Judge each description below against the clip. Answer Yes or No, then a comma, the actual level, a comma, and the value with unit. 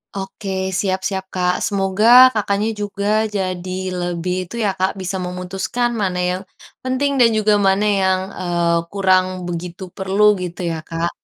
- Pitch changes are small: Yes, narrow, 1.9 semitones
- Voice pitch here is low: No, high, 190 Hz